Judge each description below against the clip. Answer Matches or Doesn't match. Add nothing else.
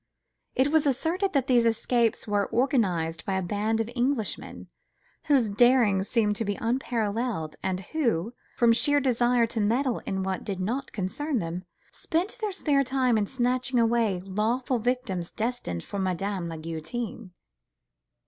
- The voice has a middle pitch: Doesn't match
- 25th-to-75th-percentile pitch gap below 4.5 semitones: Doesn't match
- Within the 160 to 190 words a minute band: Doesn't match